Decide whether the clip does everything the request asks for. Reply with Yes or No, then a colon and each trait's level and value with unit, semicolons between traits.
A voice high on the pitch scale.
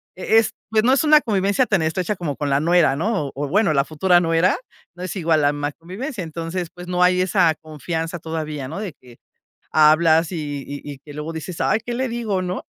No: medium, 170 Hz